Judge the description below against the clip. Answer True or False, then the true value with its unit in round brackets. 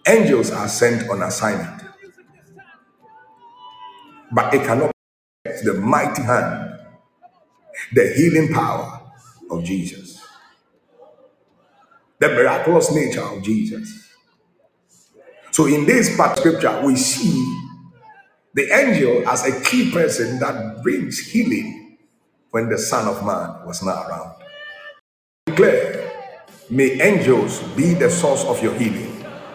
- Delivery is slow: True (110 wpm)